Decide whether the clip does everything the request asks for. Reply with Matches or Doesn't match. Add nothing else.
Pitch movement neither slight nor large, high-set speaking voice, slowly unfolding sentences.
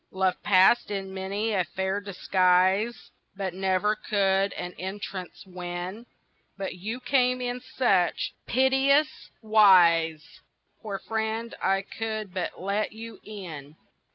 Matches